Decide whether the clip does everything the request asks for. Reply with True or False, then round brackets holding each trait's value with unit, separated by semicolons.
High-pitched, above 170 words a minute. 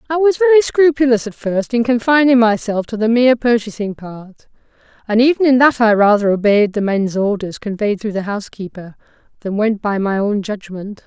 True (225 Hz; 185 wpm)